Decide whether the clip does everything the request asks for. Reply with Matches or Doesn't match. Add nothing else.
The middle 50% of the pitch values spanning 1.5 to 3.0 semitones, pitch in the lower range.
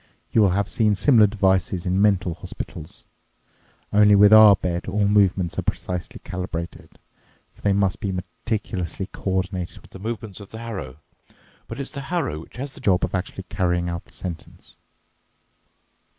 Matches